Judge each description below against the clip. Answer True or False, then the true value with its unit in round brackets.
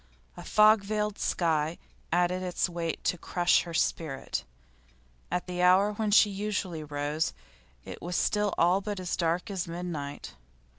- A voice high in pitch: False (180 Hz)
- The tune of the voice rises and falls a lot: False (3.2 semitones)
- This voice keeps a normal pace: True (150 wpm)